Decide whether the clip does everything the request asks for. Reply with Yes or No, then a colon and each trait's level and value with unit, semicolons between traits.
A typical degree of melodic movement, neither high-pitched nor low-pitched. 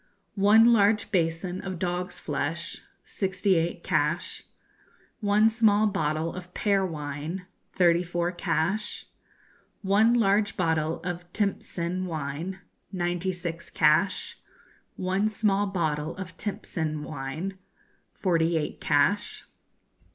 Yes: average, 3.3 semitones; medium, 180 Hz